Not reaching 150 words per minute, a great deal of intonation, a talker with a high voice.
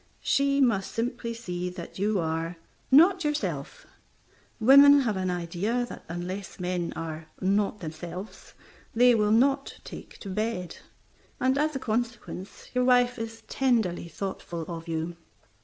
Yes: average, 140 wpm; wide, 5.9 semitones; high, 210 Hz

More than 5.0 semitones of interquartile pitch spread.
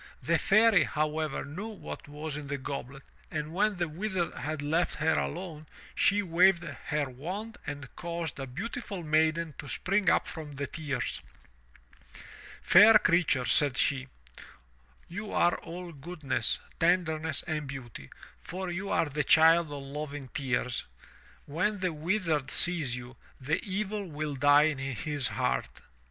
No: average, 3.8 semitones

